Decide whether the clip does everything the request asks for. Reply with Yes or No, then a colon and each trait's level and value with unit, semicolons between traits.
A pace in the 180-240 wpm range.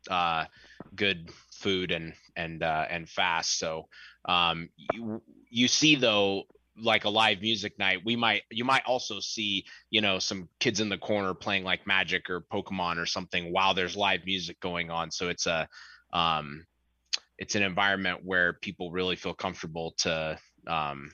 No: average, 170 wpm